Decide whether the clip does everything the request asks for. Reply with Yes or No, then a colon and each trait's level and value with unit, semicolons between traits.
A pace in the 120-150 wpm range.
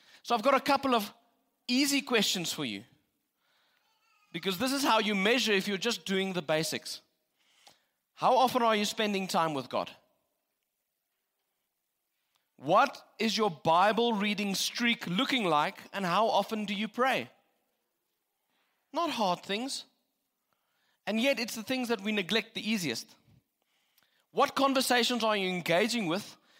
Yes: average, 140 wpm